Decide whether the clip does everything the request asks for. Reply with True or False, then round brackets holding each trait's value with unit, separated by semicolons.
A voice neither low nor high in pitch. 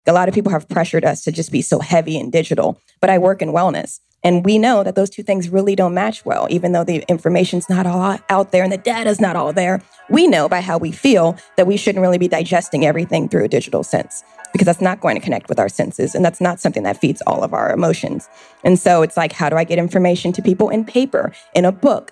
True (180 Hz)